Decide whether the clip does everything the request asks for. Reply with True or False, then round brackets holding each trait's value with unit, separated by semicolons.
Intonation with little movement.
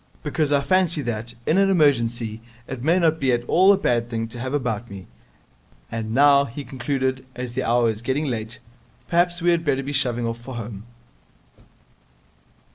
False (4.1 semitones)